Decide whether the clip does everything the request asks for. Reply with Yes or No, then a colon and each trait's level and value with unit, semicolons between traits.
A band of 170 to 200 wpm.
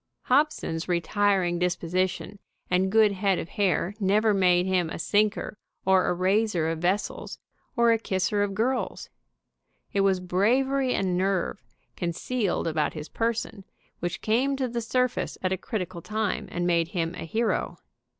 No: average, 155 wpm